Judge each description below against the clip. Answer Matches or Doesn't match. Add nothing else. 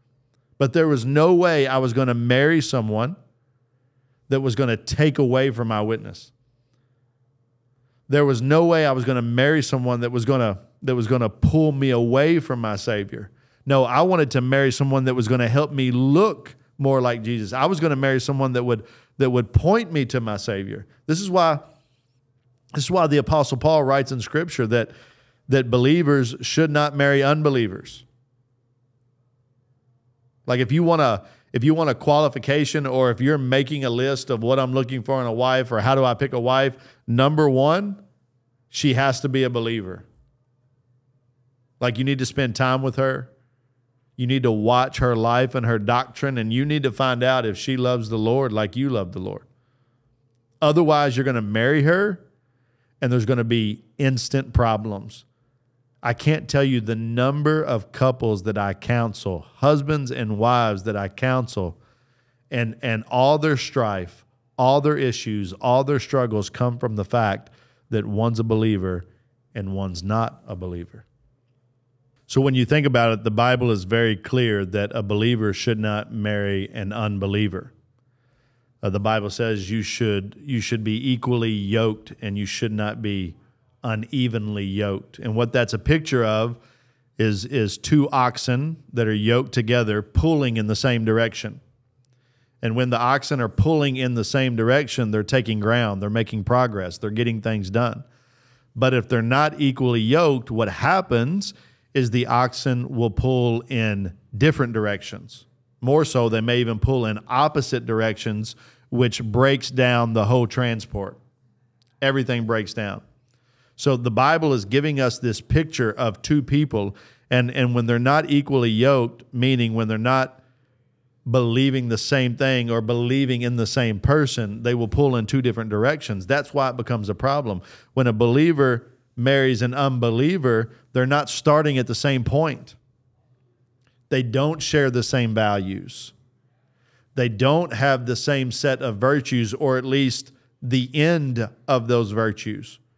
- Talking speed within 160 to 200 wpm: Matches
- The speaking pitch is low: Matches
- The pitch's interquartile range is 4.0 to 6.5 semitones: Doesn't match